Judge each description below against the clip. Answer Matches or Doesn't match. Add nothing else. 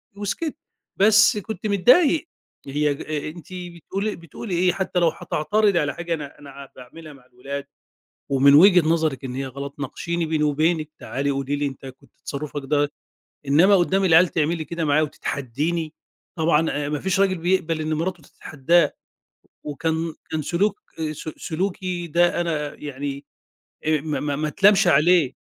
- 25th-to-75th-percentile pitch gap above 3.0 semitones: Matches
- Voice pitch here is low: Doesn't match